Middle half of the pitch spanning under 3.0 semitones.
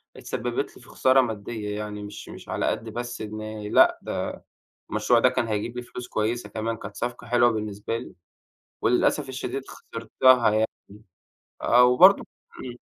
Yes: narrow, 2.4 semitones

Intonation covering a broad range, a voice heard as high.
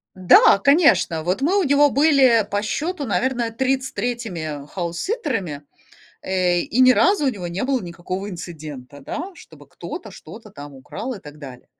Yes: wide, 7.6 semitones; high, 205 Hz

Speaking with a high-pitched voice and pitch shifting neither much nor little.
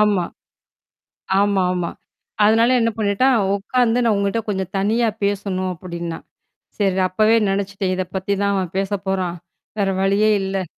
No: high, 200 Hz; narrow, 2.3 semitones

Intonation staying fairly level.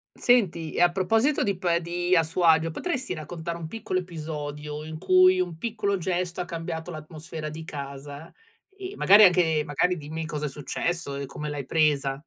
No: average, 3.1 semitones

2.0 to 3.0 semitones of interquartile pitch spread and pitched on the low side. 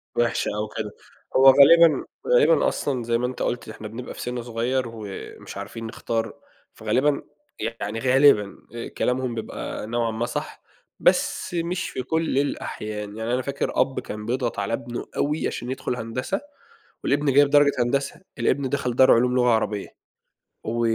No: average, 3.5 semitones; low, 125 Hz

